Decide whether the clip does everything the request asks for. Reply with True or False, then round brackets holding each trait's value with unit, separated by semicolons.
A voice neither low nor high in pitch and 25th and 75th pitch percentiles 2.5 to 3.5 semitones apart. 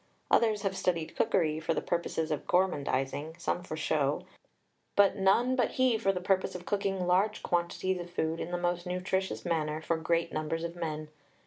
True (175 Hz; 3.1 semitones)